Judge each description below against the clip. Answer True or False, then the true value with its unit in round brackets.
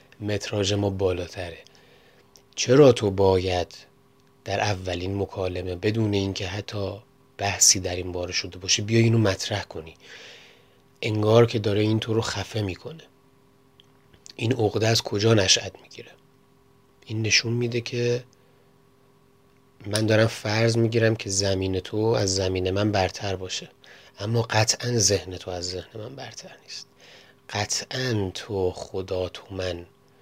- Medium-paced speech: True (130 wpm)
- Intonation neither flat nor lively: True (3.5 semitones)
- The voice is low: True (105 Hz)